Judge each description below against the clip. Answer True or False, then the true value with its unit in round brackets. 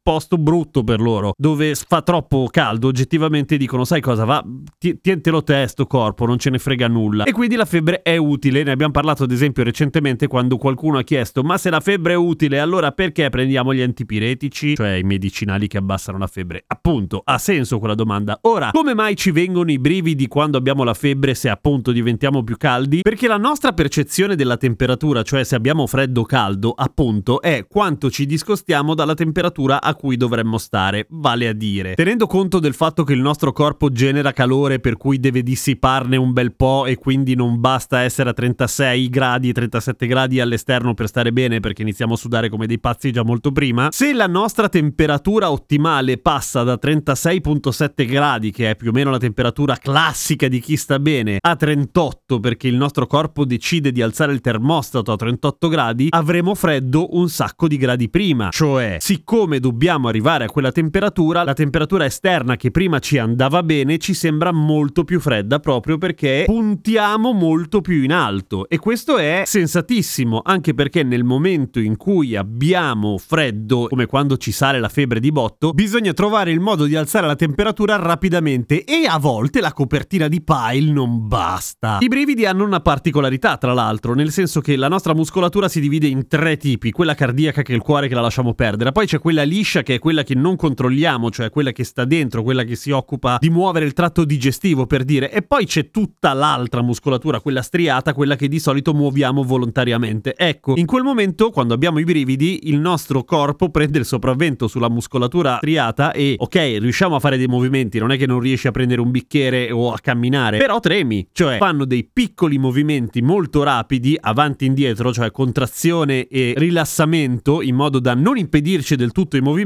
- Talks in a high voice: False (140 Hz)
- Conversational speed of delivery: False (190 wpm)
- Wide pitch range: False (4.6 semitones)